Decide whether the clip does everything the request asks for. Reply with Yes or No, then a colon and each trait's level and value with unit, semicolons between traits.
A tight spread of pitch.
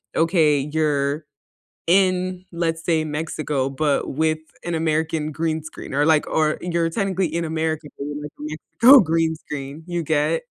Yes: narrow, 1.7 semitones